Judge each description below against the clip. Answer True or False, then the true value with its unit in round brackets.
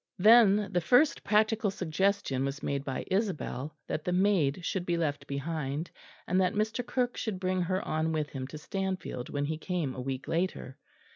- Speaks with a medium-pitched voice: True (175 Hz)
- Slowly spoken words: False (185 wpm)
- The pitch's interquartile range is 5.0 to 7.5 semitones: True (5.6 semitones)